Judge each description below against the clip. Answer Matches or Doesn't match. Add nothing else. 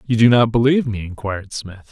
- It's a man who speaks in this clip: Matches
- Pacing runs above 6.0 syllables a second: Matches